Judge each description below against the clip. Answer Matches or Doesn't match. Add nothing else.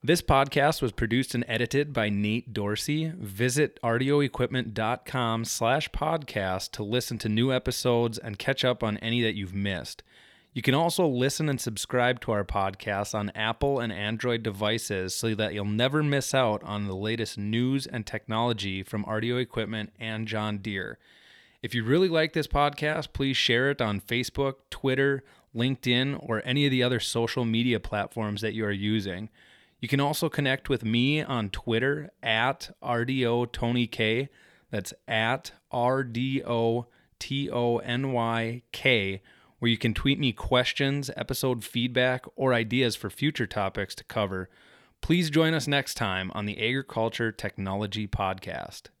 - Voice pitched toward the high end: Doesn't match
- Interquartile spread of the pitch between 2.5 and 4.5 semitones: Matches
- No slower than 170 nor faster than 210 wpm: Doesn't match